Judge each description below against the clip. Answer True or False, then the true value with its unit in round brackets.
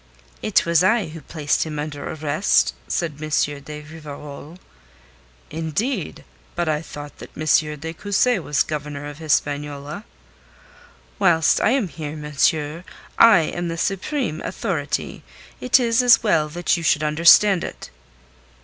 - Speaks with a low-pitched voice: False (160 Hz)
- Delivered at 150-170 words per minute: False (140 wpm)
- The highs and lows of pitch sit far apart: False (3.4 semitones)